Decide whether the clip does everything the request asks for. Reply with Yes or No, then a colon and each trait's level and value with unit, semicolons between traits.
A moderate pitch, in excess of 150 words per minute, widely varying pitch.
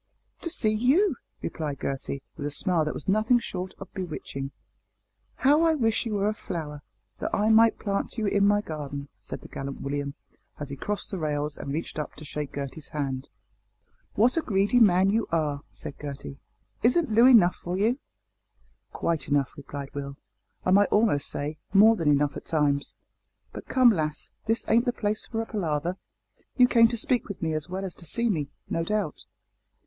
Yes: medium, 180 Hz; average, 190 wpm; wide, 7.1 semitones